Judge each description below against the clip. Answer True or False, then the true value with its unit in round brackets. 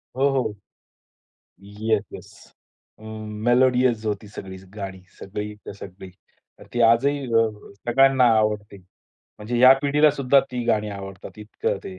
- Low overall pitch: True (110 Hz)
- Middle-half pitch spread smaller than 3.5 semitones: False (4.1 semitones)